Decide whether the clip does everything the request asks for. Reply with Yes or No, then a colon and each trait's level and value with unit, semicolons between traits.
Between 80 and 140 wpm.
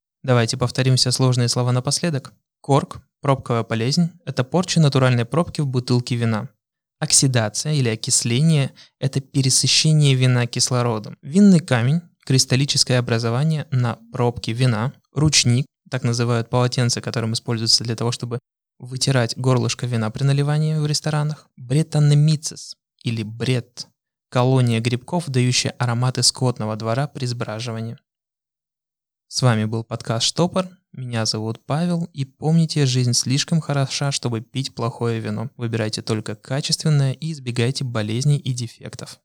Yes: average, 125 wpm